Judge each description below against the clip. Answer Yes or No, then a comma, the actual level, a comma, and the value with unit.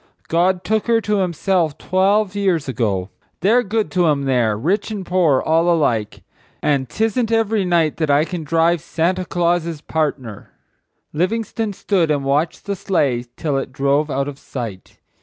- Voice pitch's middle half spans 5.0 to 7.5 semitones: Yes, wide, 5.5 semitones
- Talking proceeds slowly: No, average, 160 wpm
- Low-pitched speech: No, medium, 170 Hz